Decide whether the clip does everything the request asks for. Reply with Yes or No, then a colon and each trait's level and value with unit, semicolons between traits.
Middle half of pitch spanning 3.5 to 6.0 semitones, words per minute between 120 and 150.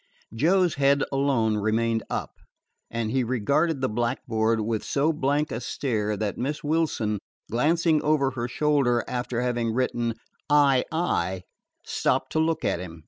Yes: average, 4.7 semitones; average, 140 wpm